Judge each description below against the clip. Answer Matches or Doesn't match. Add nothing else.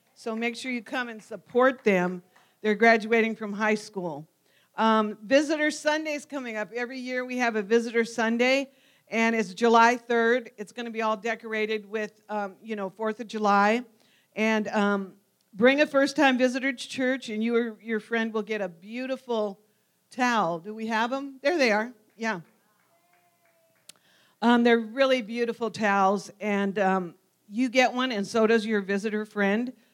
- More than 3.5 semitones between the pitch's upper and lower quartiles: Doesn't match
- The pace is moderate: Matches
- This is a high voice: Matches